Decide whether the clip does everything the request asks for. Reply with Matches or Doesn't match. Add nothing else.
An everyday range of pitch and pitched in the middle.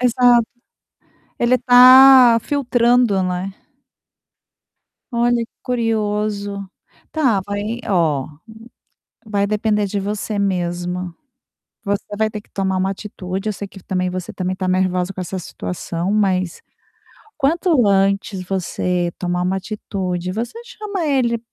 Doesn't match